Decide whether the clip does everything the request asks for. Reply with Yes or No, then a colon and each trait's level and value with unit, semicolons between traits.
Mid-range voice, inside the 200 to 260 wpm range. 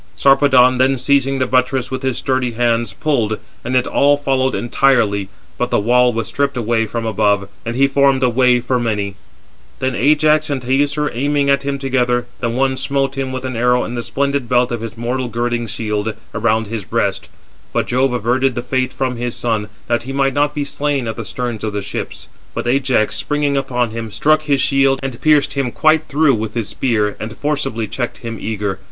No: low, 125 Hz; fast, 205 wpm